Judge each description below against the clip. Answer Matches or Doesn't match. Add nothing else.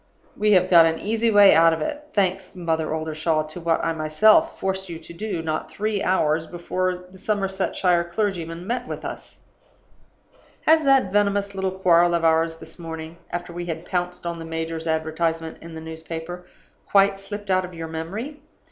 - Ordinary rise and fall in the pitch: Matches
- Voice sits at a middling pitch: Matches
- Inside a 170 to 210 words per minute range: Matches